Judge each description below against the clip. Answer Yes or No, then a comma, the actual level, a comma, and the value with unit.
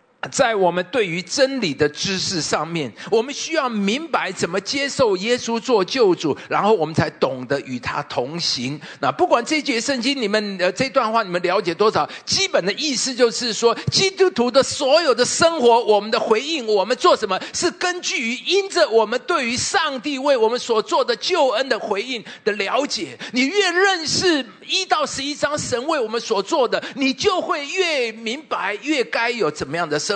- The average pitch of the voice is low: No, high, 245 Hz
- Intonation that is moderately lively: No, wide, 7.0 semitones